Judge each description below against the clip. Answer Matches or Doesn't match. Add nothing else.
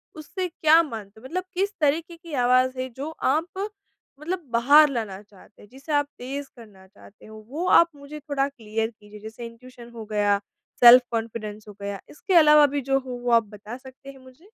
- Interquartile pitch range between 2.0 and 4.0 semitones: Doesn't match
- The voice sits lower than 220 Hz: Doesn't match